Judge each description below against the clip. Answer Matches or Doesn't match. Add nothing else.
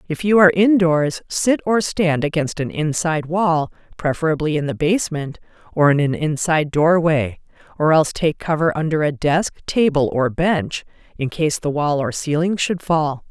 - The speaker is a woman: Matches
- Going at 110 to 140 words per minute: Doesn't match